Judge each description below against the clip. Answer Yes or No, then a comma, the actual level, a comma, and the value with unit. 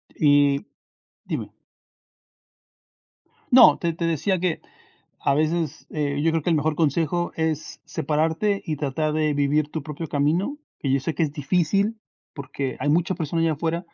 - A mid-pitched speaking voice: Yes, medium, 155 Hz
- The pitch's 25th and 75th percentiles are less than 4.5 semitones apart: Yes, narrow, 2.6 semitones